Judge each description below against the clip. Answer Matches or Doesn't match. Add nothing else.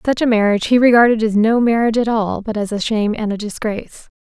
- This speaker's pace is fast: Matches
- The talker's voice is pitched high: Matches